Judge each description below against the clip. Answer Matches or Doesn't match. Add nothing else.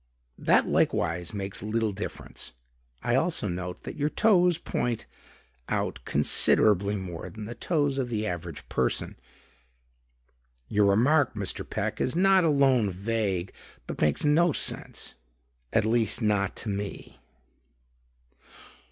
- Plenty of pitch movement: Matches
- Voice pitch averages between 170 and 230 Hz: Doesn't match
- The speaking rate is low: Matches